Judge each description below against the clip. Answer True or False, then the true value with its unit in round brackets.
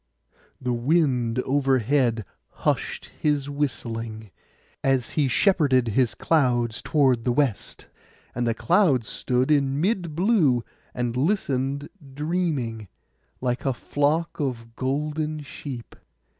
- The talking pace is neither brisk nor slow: False (110 wpm)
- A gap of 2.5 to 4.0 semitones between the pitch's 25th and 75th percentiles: True (3.7 semitones)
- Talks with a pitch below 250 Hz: True (135 Hz)